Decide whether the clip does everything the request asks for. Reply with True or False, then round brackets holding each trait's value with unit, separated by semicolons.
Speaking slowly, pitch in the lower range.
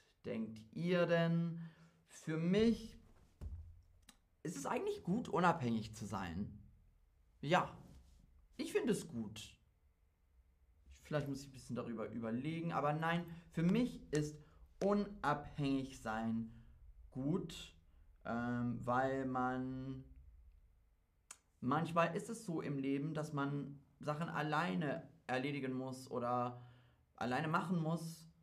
True (110 wpm; 130 Hz)